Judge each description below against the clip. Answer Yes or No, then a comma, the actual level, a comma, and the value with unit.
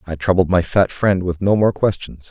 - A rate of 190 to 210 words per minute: No, fast, 235 wpm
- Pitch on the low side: Yes, very low, 90 Hz